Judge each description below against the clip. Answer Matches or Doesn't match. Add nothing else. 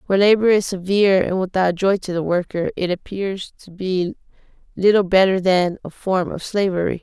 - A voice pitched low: Doesn't match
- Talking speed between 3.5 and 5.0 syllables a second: Doesn't match